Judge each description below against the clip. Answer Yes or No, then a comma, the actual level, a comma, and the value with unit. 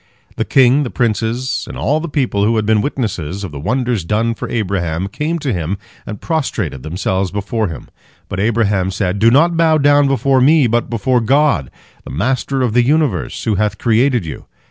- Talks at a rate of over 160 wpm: Yes, average, 190 wpm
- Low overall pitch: Yes, low, 115 Hz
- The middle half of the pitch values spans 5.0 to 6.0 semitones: Yes, wide, 5.4 semitones